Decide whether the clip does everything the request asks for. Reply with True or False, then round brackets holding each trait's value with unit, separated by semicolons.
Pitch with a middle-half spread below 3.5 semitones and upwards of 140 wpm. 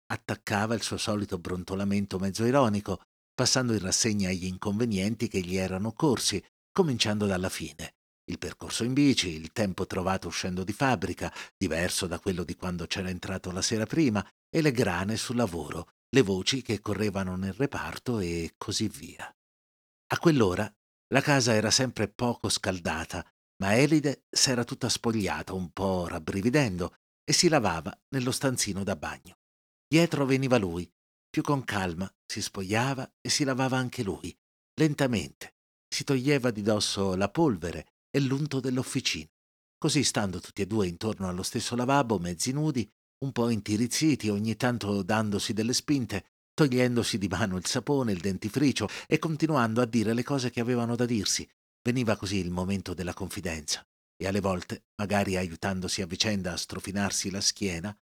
False (4.9 semitones; 155 wpm)